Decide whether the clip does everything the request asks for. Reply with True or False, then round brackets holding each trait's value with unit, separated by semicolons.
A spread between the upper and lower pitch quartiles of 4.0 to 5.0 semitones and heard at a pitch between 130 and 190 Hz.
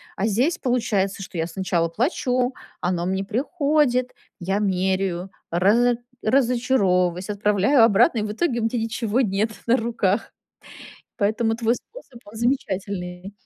False (4.3 semitones; 215 Hz)